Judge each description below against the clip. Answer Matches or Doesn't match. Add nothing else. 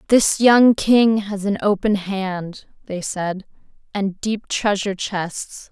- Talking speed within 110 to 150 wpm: Matches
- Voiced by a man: Doesn't match